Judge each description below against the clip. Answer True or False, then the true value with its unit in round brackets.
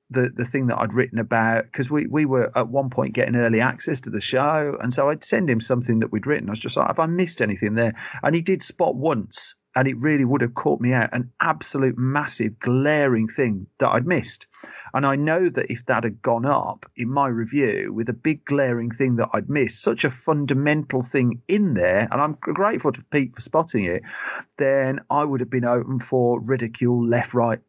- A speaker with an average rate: False (225 wpm)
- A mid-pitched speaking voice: False (130 Hz)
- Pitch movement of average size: True (3.2 semitones)